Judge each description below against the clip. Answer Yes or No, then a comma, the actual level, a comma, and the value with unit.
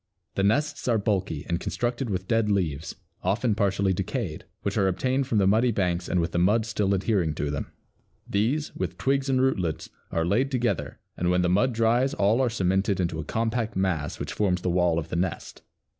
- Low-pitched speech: Yes, low, 100 Hz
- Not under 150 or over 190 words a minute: No, fast, 205 wpm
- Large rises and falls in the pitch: No, average, 4.7 semitones